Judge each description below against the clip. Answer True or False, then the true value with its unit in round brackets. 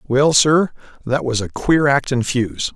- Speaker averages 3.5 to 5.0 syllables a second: True (3.9 syllables/s)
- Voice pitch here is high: False (135 Hz)